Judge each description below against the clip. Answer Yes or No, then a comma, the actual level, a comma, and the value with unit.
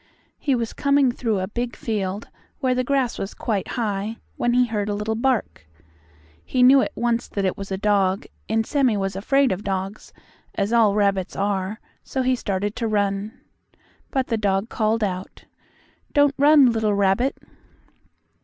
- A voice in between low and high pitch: No, high, 220 Hz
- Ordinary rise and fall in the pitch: Yes, average, 3.9 semitones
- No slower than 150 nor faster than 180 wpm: Yes, average, 170 wpm